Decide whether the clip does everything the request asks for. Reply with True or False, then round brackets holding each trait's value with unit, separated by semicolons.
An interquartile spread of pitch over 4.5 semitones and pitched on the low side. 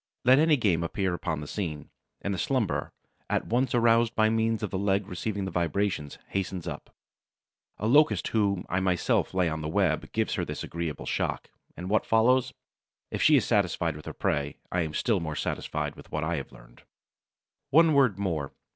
True (5.3 semitones; 95 Hz)